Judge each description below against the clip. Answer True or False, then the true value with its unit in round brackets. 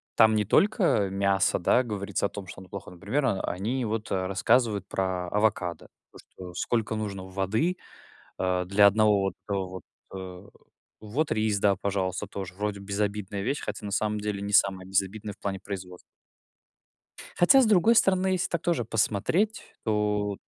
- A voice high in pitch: False (100 Hz)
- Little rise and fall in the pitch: True (2.3 semitones)